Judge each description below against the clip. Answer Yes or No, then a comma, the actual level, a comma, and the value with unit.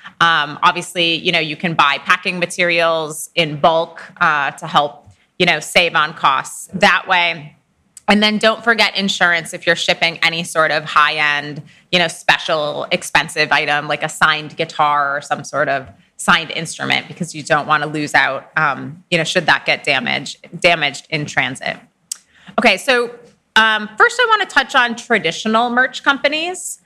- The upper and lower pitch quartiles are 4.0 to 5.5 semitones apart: Yes, average, 4.6 semitones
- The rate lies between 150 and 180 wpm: Yes, average, 170 wpm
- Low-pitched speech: No, medium, 170 Hz